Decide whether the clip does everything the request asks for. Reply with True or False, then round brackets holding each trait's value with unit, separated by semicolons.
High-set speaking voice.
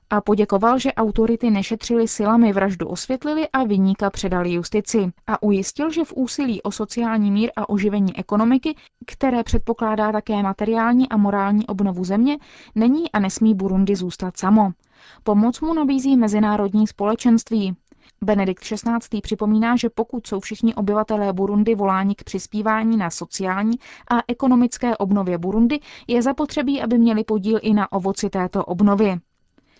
True (215 Hz)